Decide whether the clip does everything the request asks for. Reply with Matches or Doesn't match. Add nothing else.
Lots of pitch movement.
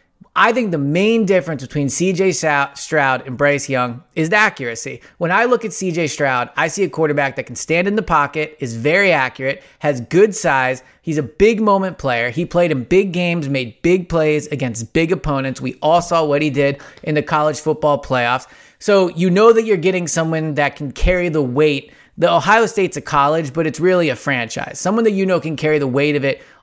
Doesn't match